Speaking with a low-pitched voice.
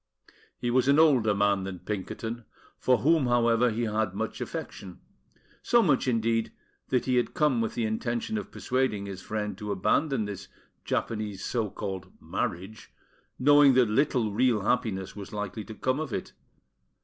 Yes: low, 115 Hz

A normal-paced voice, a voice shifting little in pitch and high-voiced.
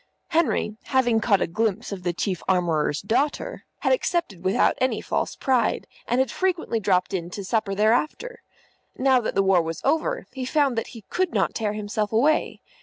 No: average, 180 wpm; wide, 5.6 semitones; high, 225 Hz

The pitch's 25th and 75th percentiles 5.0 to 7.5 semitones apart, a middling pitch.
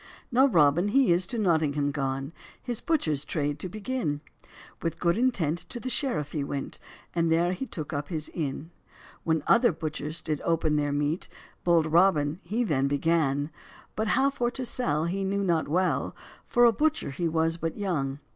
Yes: wide, 5.6 semitones; medium, 165 Hz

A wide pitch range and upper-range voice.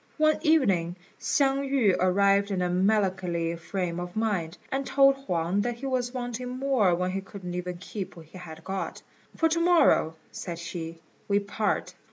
Yes: wide, 6.3 semitones; high, 195 Hz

